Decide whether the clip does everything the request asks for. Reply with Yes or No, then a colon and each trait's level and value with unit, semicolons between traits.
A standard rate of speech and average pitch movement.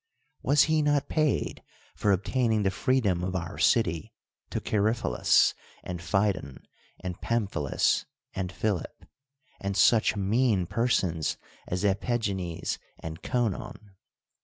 No: slow, 115 wpm; average, 4.6 semitones